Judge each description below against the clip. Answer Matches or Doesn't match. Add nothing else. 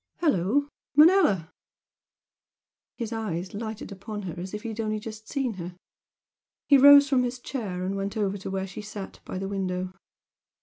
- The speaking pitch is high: Matches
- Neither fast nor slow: Matches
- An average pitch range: Matches